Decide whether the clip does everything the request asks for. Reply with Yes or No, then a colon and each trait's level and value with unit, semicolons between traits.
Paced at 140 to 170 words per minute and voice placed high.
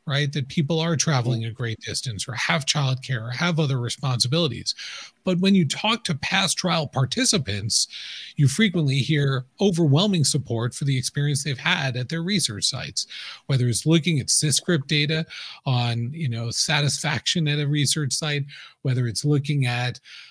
No: average, 165 wpm; medium, 145 Hz